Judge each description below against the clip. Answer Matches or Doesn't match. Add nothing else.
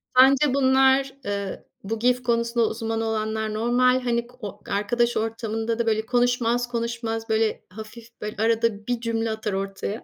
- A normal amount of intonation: Doesn't match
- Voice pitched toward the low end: Doesn't match